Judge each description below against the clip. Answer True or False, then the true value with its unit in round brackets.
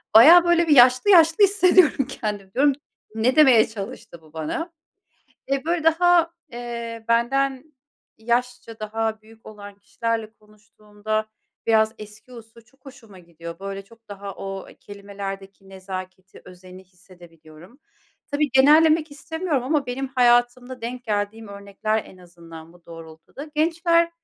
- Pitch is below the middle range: False (225 Hz)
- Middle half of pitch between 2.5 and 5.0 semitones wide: False (5.6 semitones)